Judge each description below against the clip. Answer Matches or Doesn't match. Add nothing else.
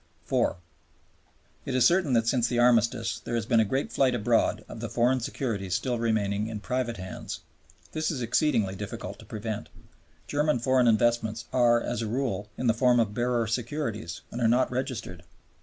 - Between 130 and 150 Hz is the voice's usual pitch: Doesn't match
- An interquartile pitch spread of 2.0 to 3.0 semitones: Matches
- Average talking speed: Matches